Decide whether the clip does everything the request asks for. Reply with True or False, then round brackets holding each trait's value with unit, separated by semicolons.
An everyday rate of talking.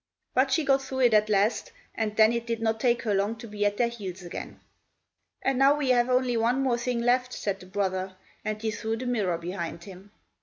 False (230 wpm)